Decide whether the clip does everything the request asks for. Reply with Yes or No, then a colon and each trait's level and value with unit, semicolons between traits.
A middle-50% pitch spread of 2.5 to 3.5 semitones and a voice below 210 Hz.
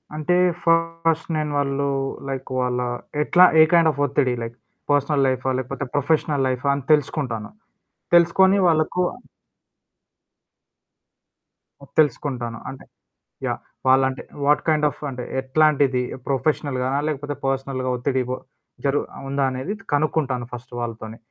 Yes: average, 3.1 semitones; medium, 140 Hz